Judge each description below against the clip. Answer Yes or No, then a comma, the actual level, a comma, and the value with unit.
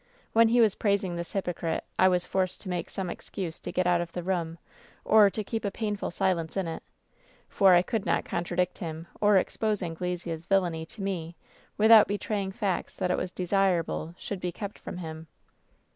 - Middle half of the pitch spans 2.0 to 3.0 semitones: Yes, average, 2.7 semitones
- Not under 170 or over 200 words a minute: Yes, average, 190 wpm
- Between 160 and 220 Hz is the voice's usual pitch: Yes, medium, 185 Hz